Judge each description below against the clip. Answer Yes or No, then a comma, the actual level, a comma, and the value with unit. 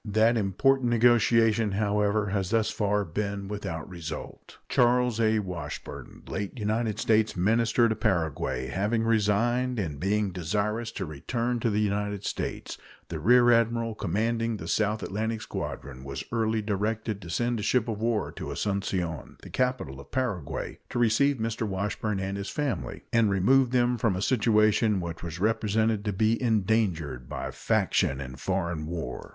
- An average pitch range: Yes, average, 3.2 semitones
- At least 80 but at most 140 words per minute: No, average, 155 wpm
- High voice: No, low, 105 Hz